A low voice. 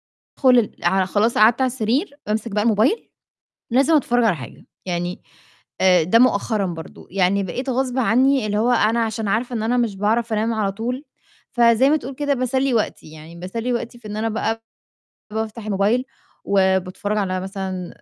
No: high, 220 Hz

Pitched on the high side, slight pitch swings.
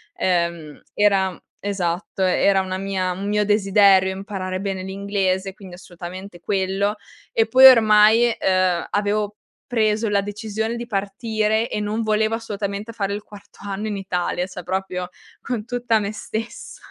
Yes: high, 200 Hz; narrow, 2.3 semitones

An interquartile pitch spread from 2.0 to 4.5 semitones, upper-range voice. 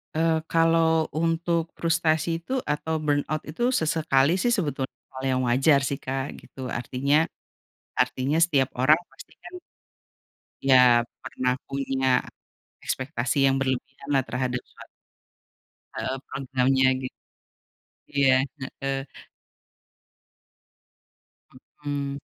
No: average, 3.5 semitones; medium, 140 Hz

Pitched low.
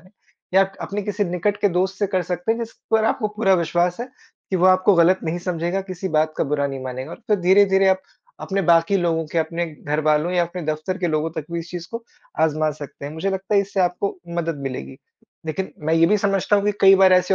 No: medium, 180 Hz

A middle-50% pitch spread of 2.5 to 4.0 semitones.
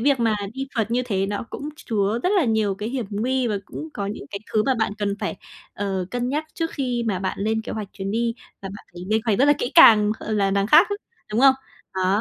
Yes: average, 3.7 semitones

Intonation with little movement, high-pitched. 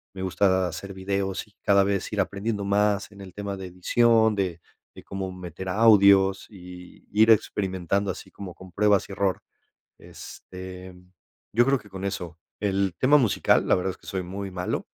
No: narrow, 1.7 semitones; very low, 95 Hz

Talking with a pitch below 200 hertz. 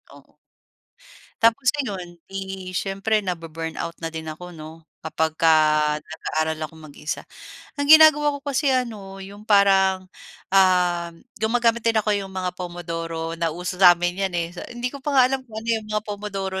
Yes: high, 190 Hz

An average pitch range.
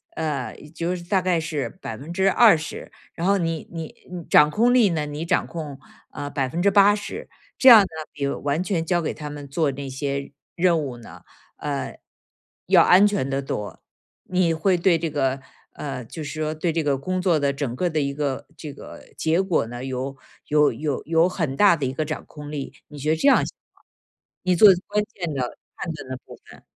Yes: average, 4.0 semitones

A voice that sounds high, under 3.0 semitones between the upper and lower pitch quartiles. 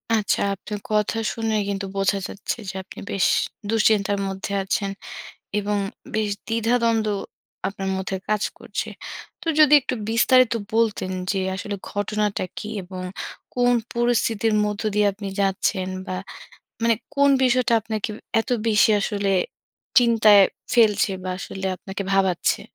Yes: high, 210 Hz; narrow, 2.6 semitones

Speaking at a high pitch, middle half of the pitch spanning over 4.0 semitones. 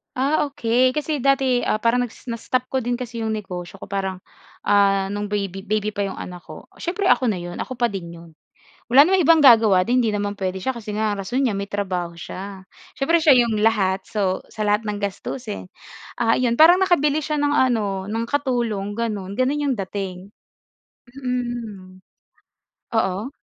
Yes: high, 220 Hz; average, 4.4 semitones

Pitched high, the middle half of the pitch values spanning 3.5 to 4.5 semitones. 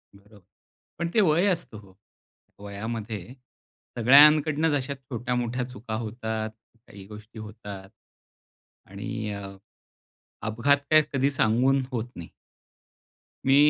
No: low, 115 Hz; average, 4.2 semitones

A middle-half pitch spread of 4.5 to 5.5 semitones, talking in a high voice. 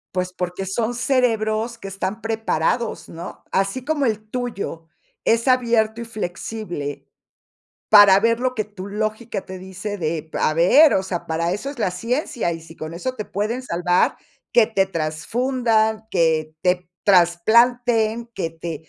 Yes: average, 4.8 semitones; high, 210 Hz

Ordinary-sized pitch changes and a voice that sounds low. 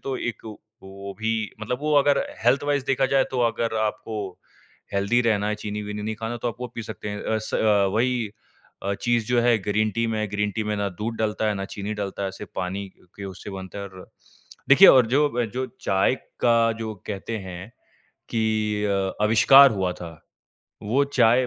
Yes: average, 3.0 semitones; low, 110 Hz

